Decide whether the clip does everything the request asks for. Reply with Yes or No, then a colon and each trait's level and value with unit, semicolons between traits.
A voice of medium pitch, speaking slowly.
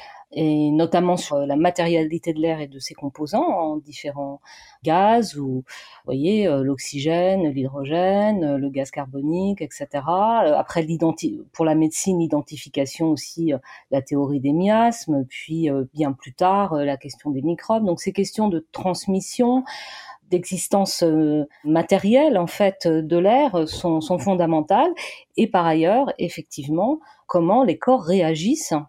Yes: medium, 165 Hz; slow, 130 wpm